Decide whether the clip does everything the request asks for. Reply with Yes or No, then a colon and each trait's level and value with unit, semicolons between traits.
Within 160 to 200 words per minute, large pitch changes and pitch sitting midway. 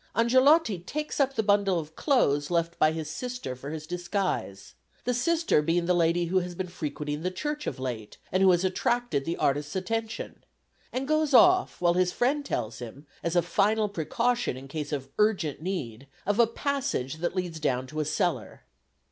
Yes: average, 190 wpm; wide, 7.6 semitones; medium, 180 Hz